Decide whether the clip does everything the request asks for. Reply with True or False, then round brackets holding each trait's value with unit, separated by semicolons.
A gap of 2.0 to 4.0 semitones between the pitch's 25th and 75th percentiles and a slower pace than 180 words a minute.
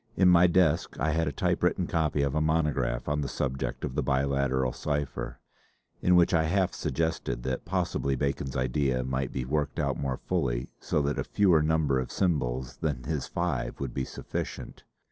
False (3.5 semitones; 185 wpm)